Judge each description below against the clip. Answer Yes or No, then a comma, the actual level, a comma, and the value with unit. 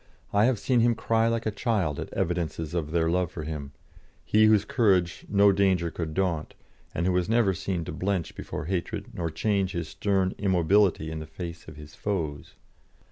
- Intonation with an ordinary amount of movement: Yes, average, 3.9 semitones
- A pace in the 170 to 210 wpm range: Yes, average, 190 wpm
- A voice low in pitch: Yes, very low, 90 Hz